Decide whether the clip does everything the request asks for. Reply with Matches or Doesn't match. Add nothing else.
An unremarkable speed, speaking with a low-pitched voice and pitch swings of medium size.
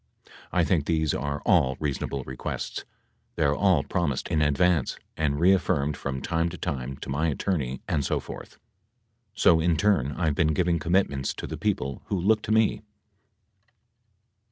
Matches